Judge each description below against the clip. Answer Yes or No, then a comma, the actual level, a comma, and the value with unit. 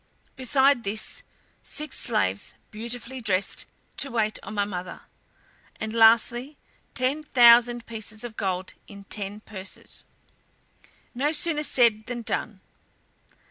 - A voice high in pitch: Yes, high, 230 Hz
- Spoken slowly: Yes, slow, 115 wpm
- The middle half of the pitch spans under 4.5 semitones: Yes, average, 3.4 semitones